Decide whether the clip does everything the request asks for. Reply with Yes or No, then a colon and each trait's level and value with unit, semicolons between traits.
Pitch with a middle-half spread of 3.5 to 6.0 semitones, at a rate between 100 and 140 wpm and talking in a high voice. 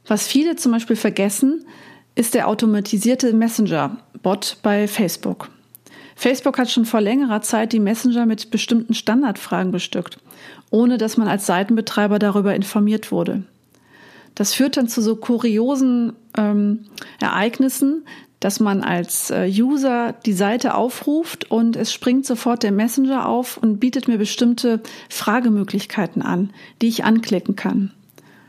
No: average, 2.7 semitones; average, 135 wpm; high, 225 Hz